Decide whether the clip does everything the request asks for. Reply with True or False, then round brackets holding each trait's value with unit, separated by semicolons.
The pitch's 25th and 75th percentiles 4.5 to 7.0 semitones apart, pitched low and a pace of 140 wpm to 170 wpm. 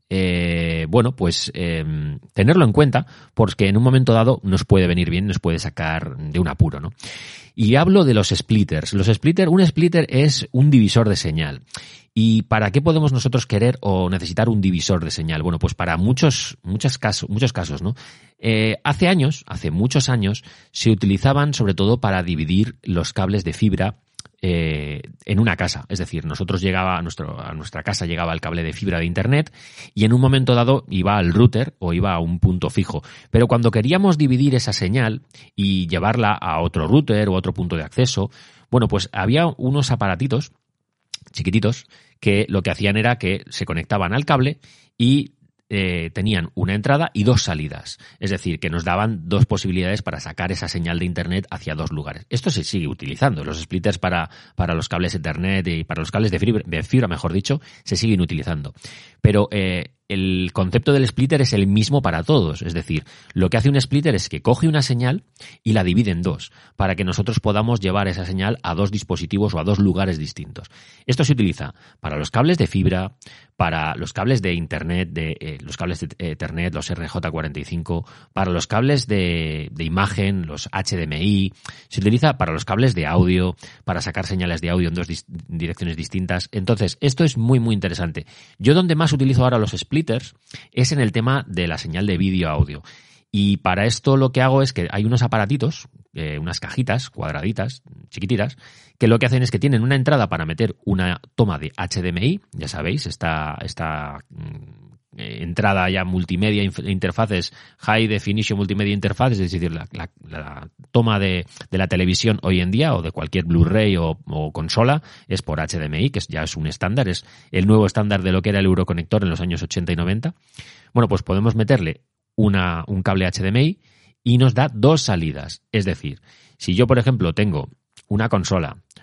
False (5.5 semitones; 100 Hz; 190 wpm)